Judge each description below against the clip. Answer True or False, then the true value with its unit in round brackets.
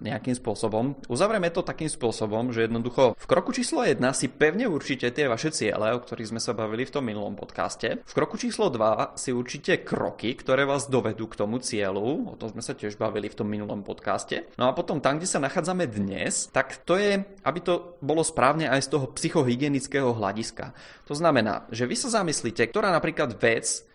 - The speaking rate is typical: False (200 wpm)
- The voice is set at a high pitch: False (135 Hz)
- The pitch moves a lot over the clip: True (6.0 semitones)